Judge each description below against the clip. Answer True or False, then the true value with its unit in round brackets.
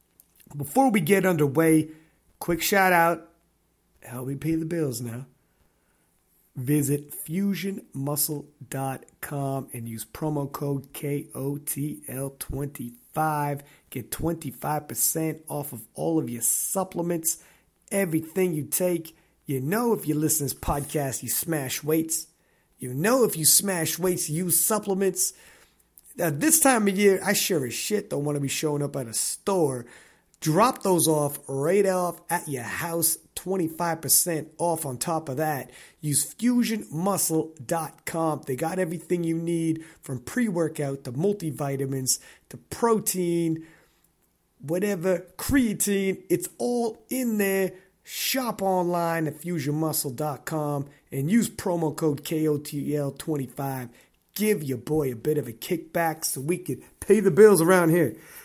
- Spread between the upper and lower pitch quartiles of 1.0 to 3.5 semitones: False (4.2 semitones)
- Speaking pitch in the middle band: True (160 Hz)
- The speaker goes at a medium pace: False (130 wpm)